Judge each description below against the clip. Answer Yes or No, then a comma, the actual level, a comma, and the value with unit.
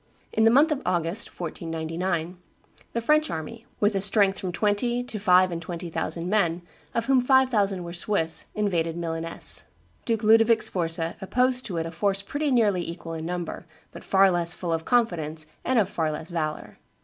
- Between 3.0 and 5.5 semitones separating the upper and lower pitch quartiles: Yes, average, 5.1 semitones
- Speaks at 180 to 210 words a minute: Yes, average, 185 wpm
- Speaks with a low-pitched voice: No, medium, 185 Hz